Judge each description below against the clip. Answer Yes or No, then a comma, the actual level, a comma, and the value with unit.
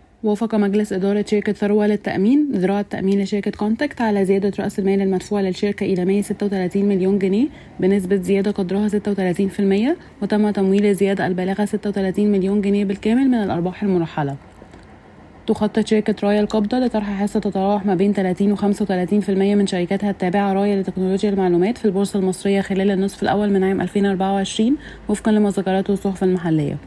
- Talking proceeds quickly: Yes, fast, 160 wpm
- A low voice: No, high, 200 Hz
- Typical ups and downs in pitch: No, narrow, 1.3 semitones